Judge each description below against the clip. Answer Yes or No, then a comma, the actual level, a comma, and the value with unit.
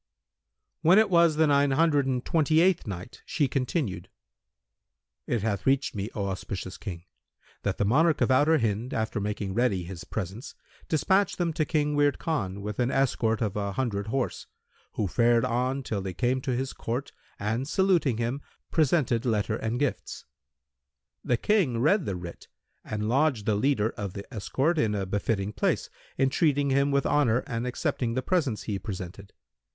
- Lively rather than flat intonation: Yes, wide, 5.7 semitones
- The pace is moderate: Yes, average, 170 wpm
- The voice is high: No, low, 125 Hz